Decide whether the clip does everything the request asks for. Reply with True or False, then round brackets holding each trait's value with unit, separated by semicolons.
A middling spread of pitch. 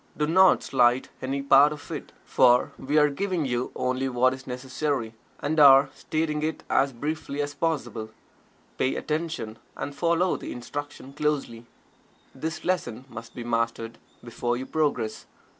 True (3.7 semitones)